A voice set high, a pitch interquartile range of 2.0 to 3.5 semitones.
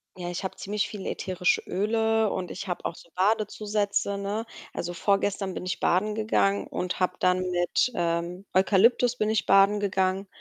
Yes: high, 195 Hz; narrow, 2.5 semitones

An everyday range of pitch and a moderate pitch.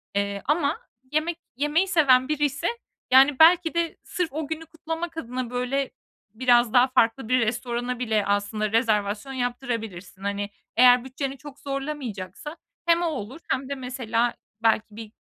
No: average, 4.8 semitones; very high, 255 Hz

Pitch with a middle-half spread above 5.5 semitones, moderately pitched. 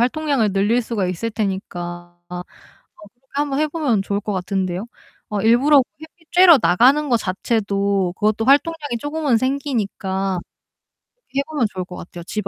No: wide, 6.5 semitones; high, 220 Hz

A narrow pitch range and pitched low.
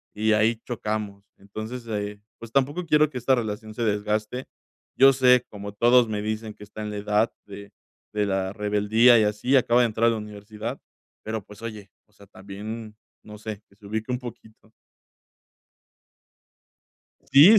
Yes: narrow, 2.2 semitones; low, 110 Hz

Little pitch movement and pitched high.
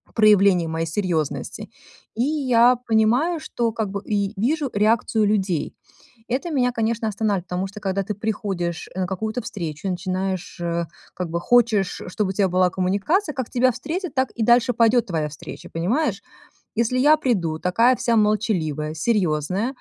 No: average, 4.8 semitones; high, 210 Hz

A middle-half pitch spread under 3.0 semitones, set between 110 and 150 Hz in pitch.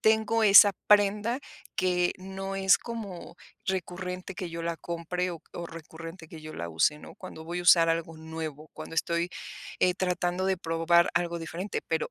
No: narrow, 2.5 semitones; medium, 175 Hz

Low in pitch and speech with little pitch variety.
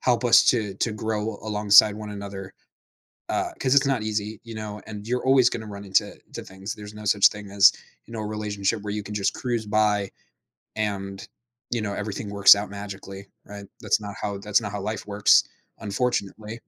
Yes: low, 105 Hz; narrow, 1.4 semitones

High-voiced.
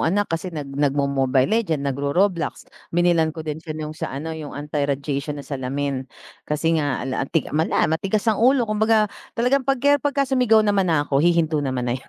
No: medium, 160 Hz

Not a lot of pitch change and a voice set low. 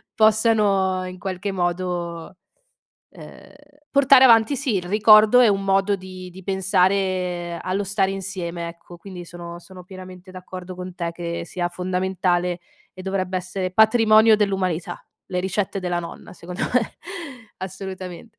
No: narrow, 1.9 semitones; medium, 185 Hz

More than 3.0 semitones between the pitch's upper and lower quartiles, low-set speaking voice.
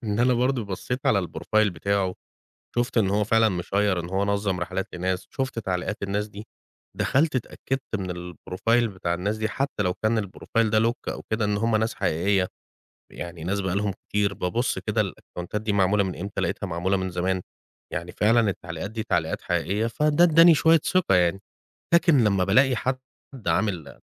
Yes: average, 3.7 semitones; low, 100 Hz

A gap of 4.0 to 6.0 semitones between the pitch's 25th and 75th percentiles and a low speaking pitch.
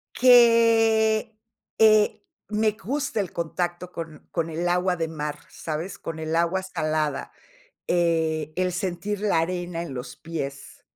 No: average, 4.6 semitones; medium, 175 Hz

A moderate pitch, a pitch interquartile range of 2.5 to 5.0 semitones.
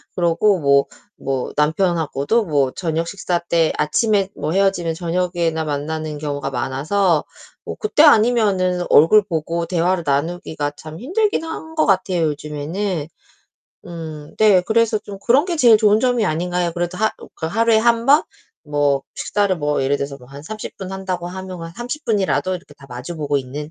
No: medium, 175 Hz; wide, 5.4 semitones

